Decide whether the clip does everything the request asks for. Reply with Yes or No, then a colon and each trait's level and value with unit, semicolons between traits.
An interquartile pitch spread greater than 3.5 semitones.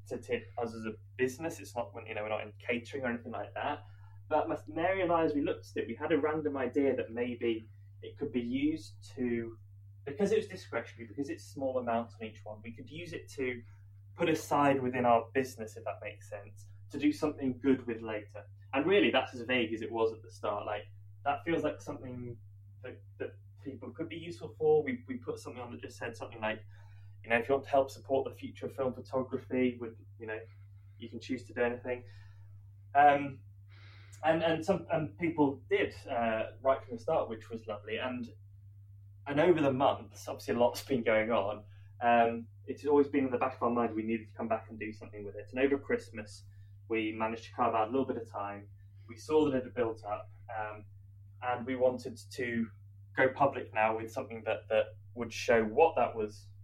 Yes: average, 4.3 semitones